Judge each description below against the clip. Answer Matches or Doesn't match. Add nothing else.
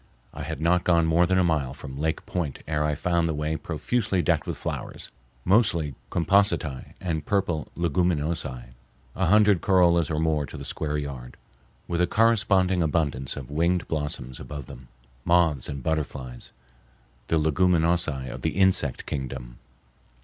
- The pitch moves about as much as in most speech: Matches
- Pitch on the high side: Doesn't match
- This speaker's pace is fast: Doesn't match